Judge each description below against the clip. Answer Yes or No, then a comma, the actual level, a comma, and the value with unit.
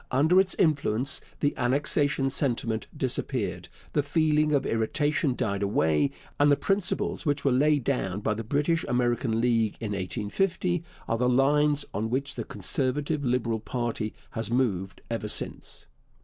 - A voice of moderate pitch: No, low, 130 Hz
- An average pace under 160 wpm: Yes, average, 150 wpm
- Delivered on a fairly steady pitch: No, average, 4.6 semitones